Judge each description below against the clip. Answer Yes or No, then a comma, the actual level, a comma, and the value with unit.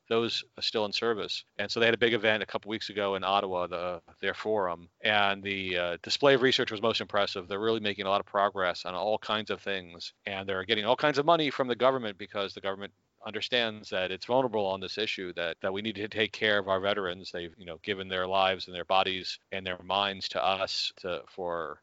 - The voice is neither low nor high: No, low, 100 Hz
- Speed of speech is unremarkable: No, fast, 245 wpm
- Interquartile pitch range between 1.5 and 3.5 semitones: Yes, average, 2.9 semitones